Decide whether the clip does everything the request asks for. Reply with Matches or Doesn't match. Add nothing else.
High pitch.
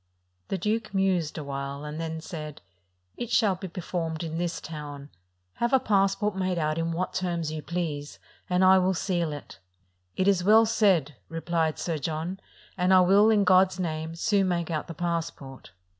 Doesn't match